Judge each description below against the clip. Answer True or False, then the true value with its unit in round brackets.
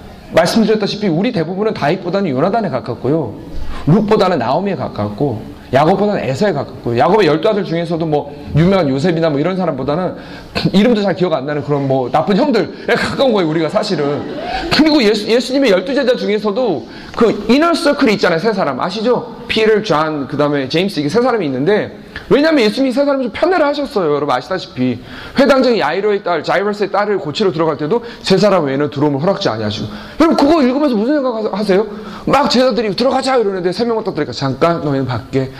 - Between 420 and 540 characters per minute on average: True (445 characters per minute)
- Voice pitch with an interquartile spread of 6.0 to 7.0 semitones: False (7.6 semitones)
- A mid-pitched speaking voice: False (195 Hz)